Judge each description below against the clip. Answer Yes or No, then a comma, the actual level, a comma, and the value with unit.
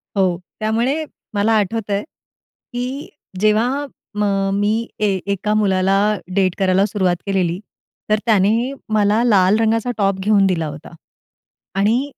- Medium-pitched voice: No, high, 210 Hz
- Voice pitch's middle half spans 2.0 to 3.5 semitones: Yes, average, 2.7 semitones